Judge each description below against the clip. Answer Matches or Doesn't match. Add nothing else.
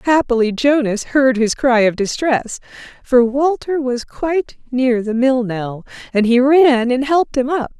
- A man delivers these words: Doesn't match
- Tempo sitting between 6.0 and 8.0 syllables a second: Doesn't match